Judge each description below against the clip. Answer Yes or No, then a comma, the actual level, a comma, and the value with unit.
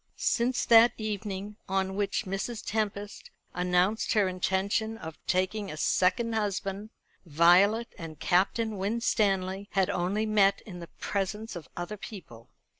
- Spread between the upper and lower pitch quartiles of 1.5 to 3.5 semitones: Yes, average, 2.7 semitones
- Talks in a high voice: Yes, high, 195 Hz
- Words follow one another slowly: Yes, slow, 130 wpm